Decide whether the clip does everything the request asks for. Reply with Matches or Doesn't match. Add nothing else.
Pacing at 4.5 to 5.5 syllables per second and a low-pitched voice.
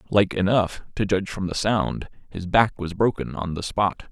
Matches